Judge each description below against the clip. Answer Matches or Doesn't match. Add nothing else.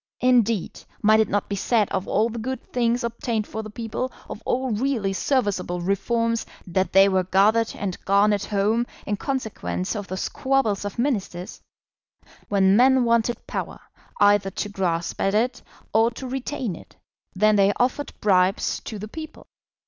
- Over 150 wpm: Matches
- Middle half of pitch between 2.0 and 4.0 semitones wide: Matches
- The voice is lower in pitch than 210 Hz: Doesn't match